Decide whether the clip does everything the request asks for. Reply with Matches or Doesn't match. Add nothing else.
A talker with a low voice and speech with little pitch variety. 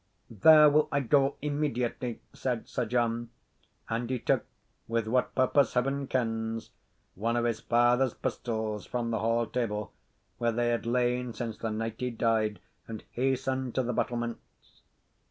Matches